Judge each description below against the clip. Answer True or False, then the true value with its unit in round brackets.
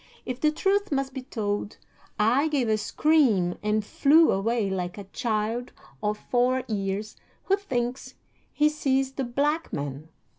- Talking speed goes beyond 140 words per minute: True (150 wpm)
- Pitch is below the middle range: False (245 Hz)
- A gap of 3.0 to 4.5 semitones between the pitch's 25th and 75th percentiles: False (5.2 semitones)